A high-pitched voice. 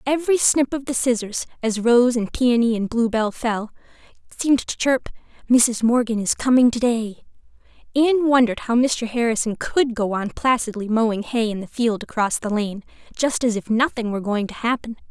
Yes: high, 235 Hz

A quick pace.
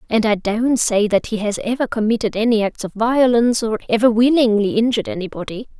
No: average, 185 wpm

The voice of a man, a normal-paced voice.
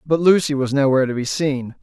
No: male; fast, 230 wpm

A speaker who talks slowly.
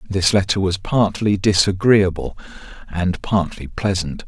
Yes: slow, 110 wpm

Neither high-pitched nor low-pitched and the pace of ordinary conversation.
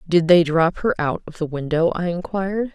No: medium, 170 Hz; fast, 220 wpm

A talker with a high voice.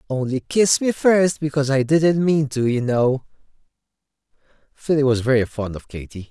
No: medium, 140 Hz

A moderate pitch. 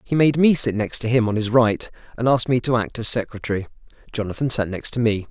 No: low, 115 Hz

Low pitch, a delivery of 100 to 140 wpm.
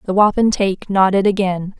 No: high, 195 Hz; slow, 135 wpm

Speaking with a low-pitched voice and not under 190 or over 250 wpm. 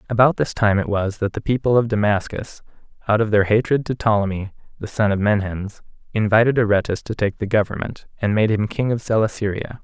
Yes: low, 105 Hz; average, 195 wpm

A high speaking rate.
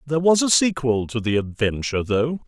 No: average, 195 wpm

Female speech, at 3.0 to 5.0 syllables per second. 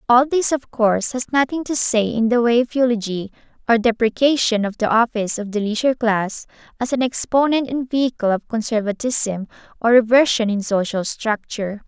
No: female; 5.4 syllables/s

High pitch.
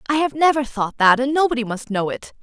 Yes: very high, 255 Hz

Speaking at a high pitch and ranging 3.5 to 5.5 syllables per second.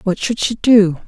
Yes: high, 205 Hz; 4.3 syllables/s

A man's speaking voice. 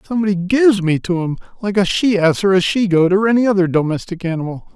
Yes: male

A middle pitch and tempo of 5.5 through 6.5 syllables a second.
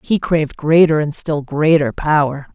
No: medium, 150 Hz; 4.6 syllables/s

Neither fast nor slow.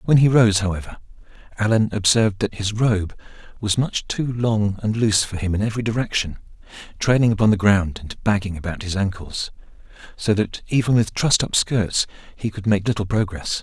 Yes: average, 180 wpm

